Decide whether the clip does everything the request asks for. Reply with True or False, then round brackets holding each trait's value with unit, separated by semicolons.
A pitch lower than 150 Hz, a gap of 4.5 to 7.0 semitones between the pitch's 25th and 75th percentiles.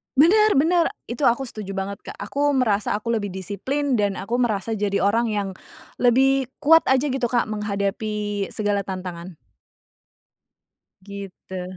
False (215 Hz; 4.8 semitones)